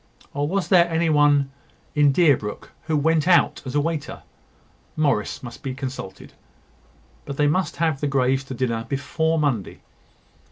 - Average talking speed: Yes, average, 155 wpm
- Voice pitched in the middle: Yes, medium, 145 Hz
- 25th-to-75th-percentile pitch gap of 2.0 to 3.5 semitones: Yes, average, 3.2 semitones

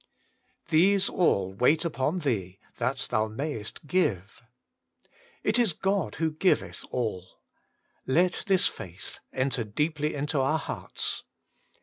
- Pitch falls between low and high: Yes, medium, 145 Hz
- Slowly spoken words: Yes, slow, 125 wpm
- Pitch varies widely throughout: Yes, wide, 8.0 semitones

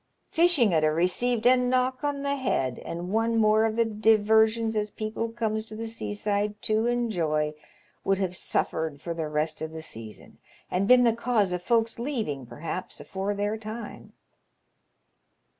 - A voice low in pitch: No, high, 215 Hz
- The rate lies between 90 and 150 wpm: No, average, 165 wpm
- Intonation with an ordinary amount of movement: Yes, average, 4.6 semitones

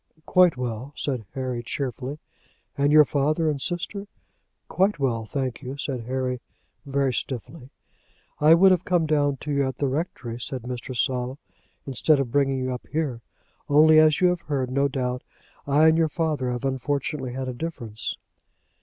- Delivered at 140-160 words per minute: No, average, 170 wpm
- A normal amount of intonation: Yes, average, 3.3 semitones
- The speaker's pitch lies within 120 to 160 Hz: Yes, medium, 140 Hz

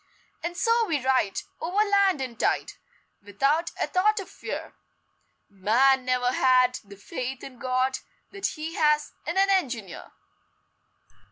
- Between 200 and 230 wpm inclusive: No, average, 140 wpm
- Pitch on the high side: Yes, very high, 270 Hz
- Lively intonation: Yes, wide, 6.3 semitones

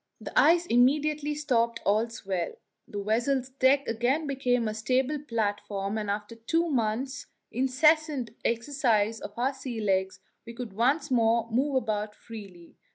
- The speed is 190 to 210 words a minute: No, average, 145 wpm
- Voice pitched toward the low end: No, high, 235 Hz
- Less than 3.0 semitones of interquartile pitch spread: No, average, 4.2 semitones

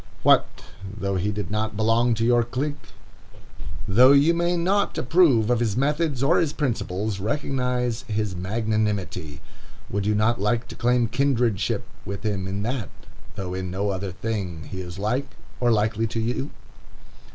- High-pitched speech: No, low, 110 Hz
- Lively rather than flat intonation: No, average, 4.0 semitones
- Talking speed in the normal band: Yes, average, 160 wpm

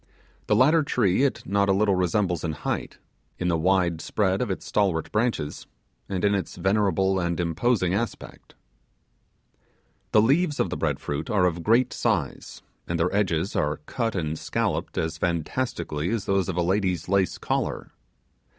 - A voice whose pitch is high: No, very low, 95 Hz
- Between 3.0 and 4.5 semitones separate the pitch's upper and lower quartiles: Yes, average, 3.8 semitones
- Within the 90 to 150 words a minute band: No, average, 165 wpm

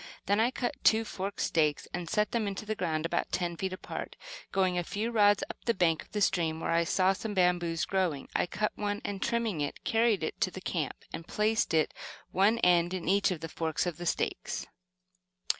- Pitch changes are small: No, average, 3.8 semitones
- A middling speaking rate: No, fast, 215 wpm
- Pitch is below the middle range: No, medium, 185 Hz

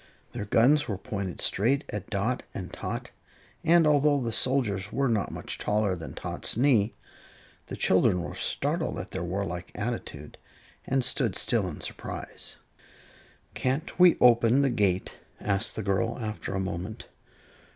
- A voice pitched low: Yes, low, 110 Hz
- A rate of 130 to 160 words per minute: Yes, average, 150 wpm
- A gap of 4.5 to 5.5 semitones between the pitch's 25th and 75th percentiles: Yes, average, 4.9 semitones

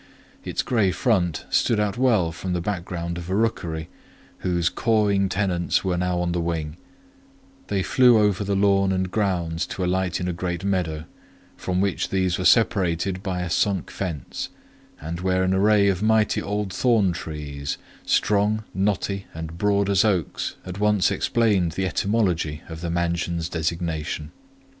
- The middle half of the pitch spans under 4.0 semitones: Yes, average, 2.8 semitones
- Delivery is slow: No, average, 160 wpm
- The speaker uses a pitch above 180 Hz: No, very low, 95 Hz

